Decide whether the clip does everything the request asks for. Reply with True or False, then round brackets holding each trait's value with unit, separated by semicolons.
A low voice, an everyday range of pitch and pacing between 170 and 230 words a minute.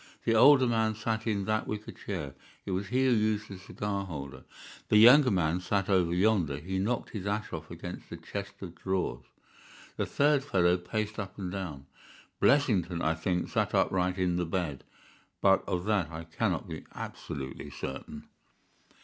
True (95 Hz; 3.7 semitones; 175 wpm)